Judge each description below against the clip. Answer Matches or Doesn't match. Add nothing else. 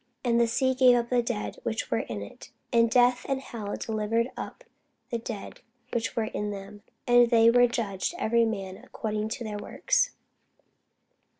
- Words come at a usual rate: Matches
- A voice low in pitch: Doesn't match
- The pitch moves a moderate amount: Doesn't match